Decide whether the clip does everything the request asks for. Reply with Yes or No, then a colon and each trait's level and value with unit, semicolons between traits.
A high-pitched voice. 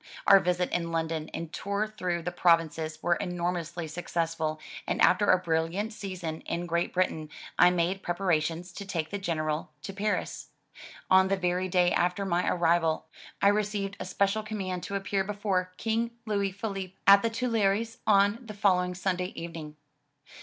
No: medium, 180 Hz